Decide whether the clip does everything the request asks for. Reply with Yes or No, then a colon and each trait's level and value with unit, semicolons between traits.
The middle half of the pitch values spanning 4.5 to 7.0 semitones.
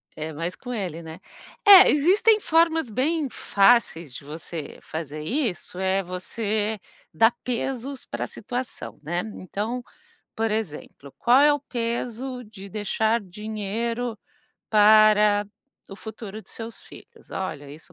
Yes: average, 5.1 semitones